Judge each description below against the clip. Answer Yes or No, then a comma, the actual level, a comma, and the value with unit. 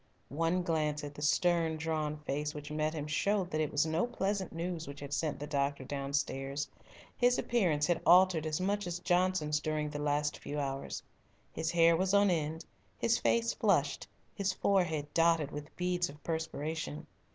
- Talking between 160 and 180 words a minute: Yes, average, 175 wpm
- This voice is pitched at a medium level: Yes, medium, 160 Hz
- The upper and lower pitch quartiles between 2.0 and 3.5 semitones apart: Yes, average, 3.2 semitones